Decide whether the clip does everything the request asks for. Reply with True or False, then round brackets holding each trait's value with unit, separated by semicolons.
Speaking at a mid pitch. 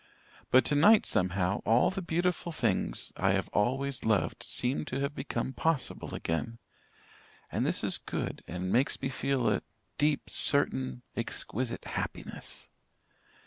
False (130 Hz)